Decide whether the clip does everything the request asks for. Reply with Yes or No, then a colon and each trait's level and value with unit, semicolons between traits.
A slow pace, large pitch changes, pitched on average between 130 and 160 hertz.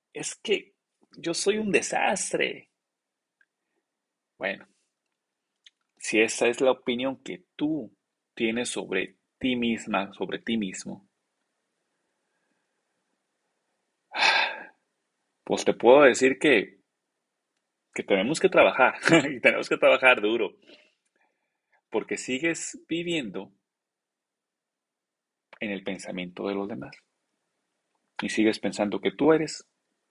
No: slow, 100 wpm; wide, 7.8 semitones; low, 120 Hz